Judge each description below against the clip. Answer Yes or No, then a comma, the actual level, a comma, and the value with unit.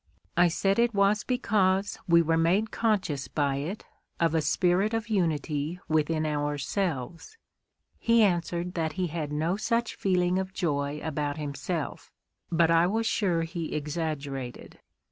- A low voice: No, medium, 170 Hz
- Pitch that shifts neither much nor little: Yes, average, 4.3 semitones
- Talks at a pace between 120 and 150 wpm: Yes, average, 145 wpm